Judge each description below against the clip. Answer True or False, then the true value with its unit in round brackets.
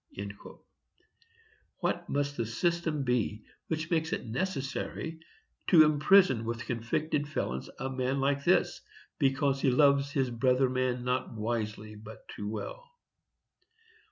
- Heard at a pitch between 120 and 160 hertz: True (135 Hz)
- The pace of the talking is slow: True (125 wpm)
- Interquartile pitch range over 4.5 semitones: False (4.0 semitones)